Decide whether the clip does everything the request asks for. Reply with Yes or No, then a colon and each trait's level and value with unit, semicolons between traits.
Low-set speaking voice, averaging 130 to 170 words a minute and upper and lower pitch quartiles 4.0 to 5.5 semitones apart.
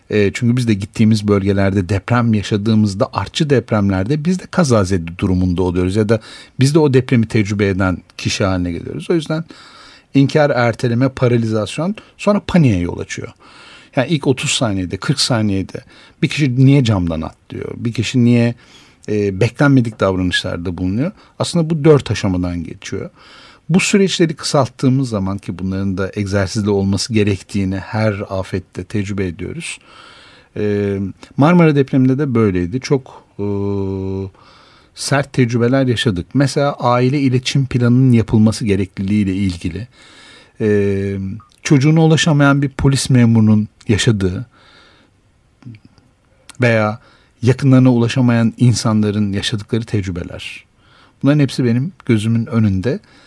No: low, 115 Hz; average, 120 wpm; average, 5.2 semitones